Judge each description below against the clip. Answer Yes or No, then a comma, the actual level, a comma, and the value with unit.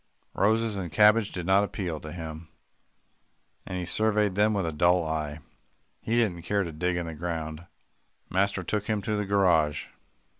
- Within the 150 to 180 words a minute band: Yes, average, 175 wpm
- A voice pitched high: No, very low, 90 Hz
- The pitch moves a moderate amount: Yes, average, 4.1 semitones